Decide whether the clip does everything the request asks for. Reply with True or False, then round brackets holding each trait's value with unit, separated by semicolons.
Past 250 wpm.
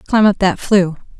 False (200 wpm)